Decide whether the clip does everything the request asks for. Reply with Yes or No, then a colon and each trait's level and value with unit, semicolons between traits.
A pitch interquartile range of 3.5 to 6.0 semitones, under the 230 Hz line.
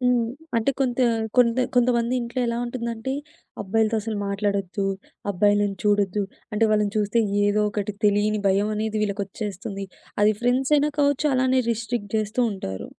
No: average, 2.8 semitones; high, 215 Hz